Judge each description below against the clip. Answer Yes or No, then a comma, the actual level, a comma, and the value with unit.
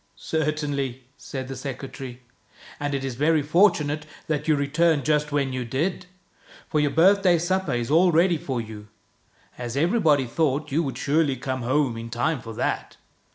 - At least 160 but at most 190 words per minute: Yes, average, 180 wpm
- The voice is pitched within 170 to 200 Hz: No, medium, 145 Hz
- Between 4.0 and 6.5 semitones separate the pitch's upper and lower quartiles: No, average, 3.5 semitones